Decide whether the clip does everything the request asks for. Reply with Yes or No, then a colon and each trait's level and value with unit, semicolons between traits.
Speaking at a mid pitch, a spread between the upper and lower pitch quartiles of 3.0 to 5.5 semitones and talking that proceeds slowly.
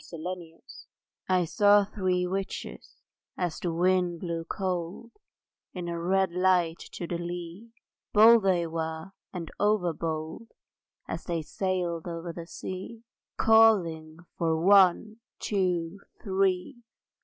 No: medium, 180 Hz; narrow, 2.4 semitones; slow, 125 wpm